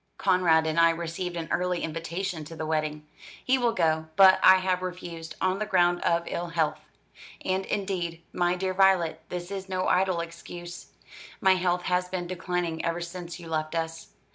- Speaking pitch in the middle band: Yes, medium, 175 Hz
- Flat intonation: Yes, narrow, 1.9 semitones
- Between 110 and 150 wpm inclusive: No, average, 180 wpm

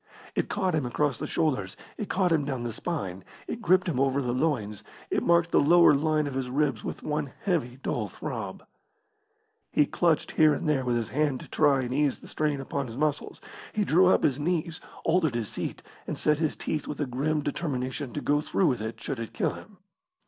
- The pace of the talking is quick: Yes, fast, 215 wpm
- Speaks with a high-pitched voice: No, medium, 145 Hz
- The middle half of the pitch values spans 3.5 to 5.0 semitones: Yes, average, 3.8 semitones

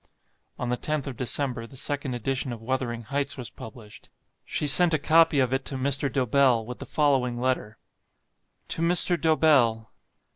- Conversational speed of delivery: Yes, average, 170 wpm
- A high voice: No, low, 130 Hz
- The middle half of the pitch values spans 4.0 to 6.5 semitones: No, average, 3.0 semitones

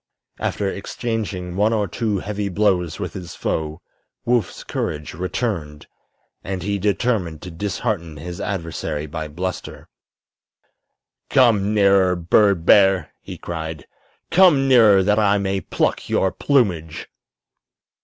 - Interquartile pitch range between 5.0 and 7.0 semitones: No, average, 3.8 semitones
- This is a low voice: Yes, very low, 95 Hz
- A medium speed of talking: No, slow, 120 wpm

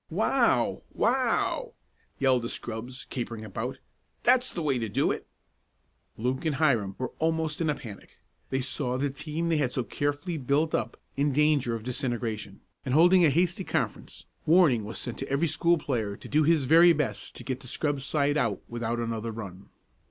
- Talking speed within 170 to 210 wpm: Yes, average, 180 wpm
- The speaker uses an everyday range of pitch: Yes, average, 5.0 semitones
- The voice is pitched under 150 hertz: Yes, low, 135 Hz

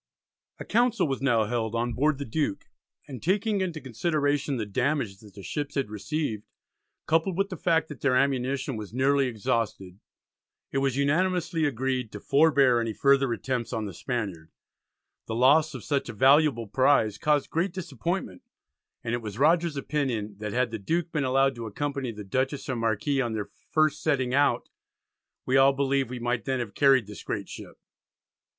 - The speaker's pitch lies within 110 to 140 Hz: Yes, low, 135 Hz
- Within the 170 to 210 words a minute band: Yes, average, 180 wpm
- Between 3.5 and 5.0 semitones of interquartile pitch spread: Yes, average, 4.4 semitones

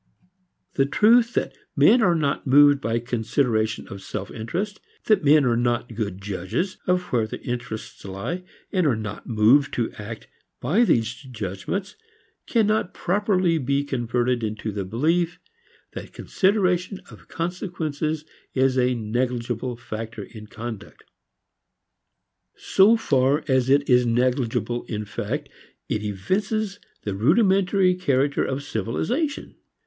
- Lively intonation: Yes, wide, 7.9 semitones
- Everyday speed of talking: No, slow, 130 wpm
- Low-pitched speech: Yes, low, 130 Hz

